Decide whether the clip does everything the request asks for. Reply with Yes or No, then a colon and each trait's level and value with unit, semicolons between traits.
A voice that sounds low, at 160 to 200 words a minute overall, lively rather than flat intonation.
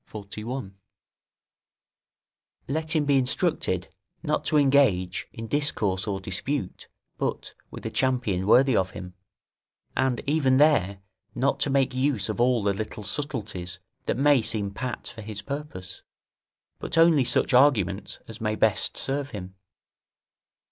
No: low, 120 Hz; slow, 135 wpm; wide, 5.8 semitones